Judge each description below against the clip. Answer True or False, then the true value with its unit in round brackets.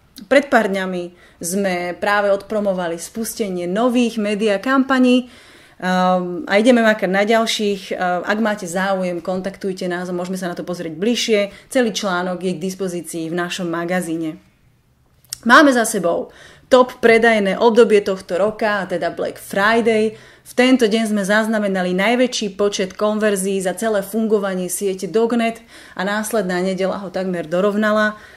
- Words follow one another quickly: False (140 wpm)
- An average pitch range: True (3.5 semitones)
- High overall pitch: True (200 Hz)